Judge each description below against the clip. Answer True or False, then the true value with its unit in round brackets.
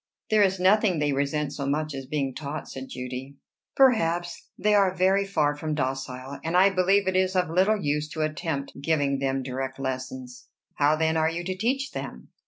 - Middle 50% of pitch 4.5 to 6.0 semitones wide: True (5.2 semitones)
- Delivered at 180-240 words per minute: True (190 wpm)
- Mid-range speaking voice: True (155 Hz)